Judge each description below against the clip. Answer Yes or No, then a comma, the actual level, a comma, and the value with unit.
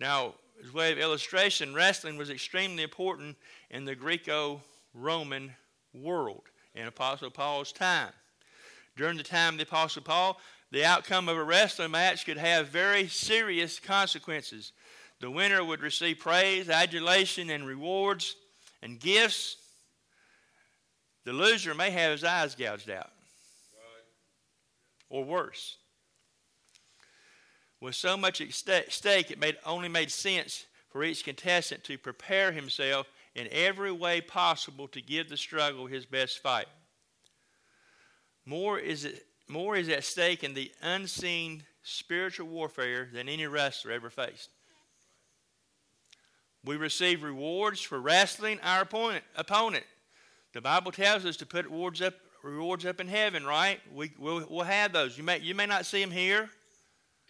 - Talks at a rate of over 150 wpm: No, average, 140 wpm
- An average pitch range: Yes, average, 4.3 semitones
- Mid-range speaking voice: Yes, medium, 165 Hz